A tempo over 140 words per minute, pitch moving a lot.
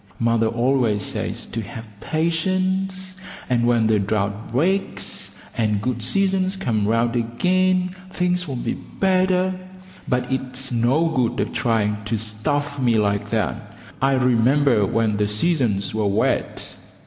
No: slow, 135 wpm; wide, 7.4 semitones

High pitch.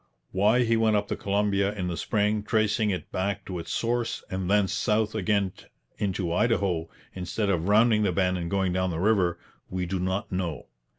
No: low, 100 Hz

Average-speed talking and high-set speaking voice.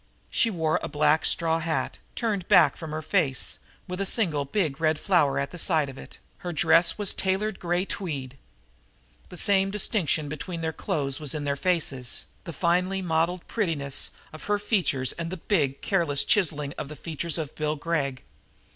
No: average, 180 wpm; medium, 165 Hz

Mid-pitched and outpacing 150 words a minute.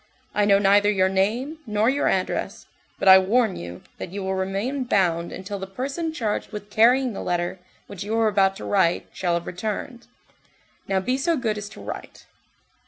No: high, 205 Hz; average, 190 wpm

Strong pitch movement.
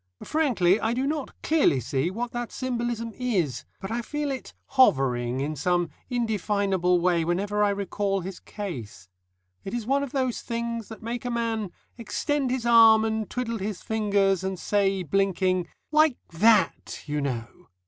No: average, 4.9 semitones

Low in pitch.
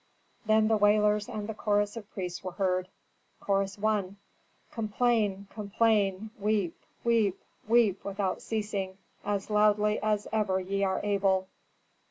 No: high, 205 Hz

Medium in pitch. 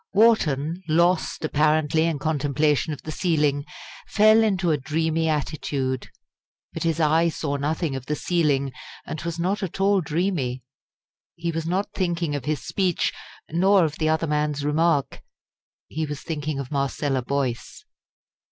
Yes: medium, 155 Hz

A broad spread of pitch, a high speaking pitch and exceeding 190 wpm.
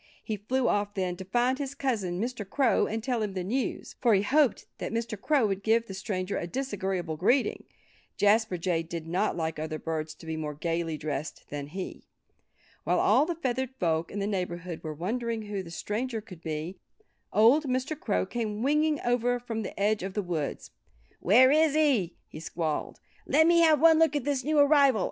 Yes: wide, 6.7 semitones; high, 210 Hz; average, 200 wpm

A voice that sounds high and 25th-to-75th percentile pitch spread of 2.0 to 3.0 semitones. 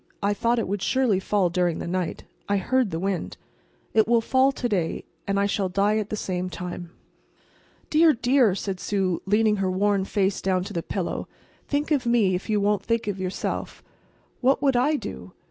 No: high, 205 Hz; average, 4.0 semitones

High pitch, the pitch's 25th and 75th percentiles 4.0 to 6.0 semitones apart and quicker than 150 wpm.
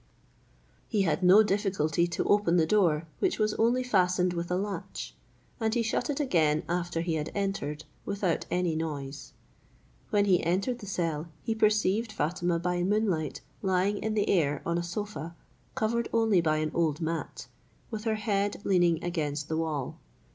No: medium, 180 Hz; average, 4.3 semitones; average, 170 wpm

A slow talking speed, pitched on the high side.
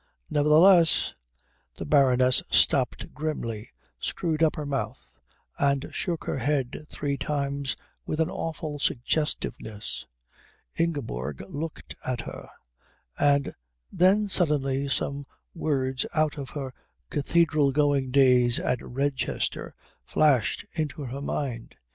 No: slow, 110 wpm; medium, 140 Hz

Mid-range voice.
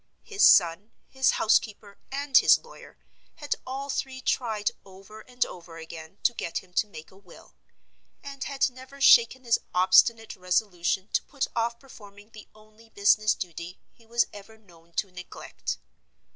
No: high, 215 Hz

